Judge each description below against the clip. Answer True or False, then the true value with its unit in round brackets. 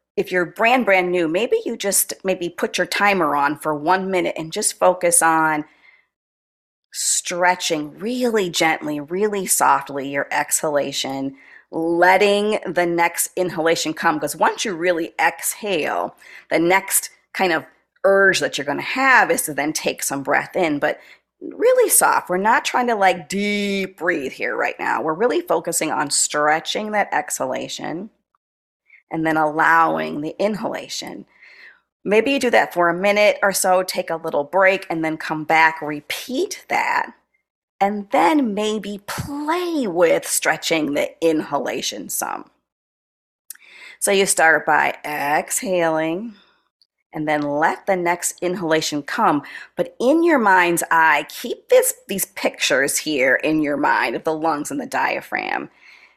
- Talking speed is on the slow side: False (145 wpm)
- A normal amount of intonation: True (4.8 semitones)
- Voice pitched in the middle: True (180 Hz)